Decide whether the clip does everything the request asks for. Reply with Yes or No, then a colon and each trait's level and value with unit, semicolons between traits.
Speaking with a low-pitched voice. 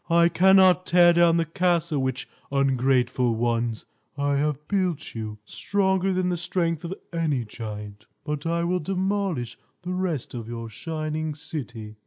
No: medium, 155 Hz